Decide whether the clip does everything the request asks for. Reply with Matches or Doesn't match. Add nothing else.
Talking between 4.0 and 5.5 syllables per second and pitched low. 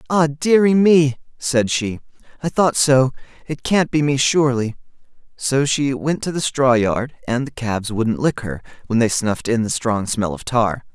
Matches